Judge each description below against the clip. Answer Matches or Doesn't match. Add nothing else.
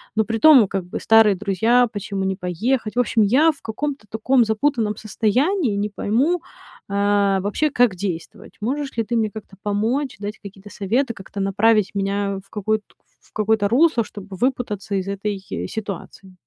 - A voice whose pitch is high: Matches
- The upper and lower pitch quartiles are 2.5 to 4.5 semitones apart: Matches